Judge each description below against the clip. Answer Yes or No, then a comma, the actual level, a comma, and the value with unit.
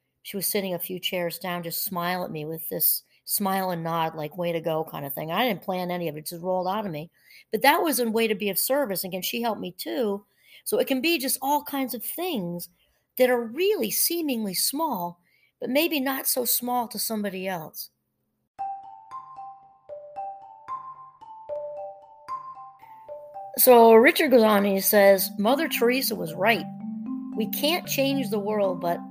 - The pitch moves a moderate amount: No, wide, 7.2 semitones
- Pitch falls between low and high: No, high, 225 Hz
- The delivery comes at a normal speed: Yes, average, 180 wpm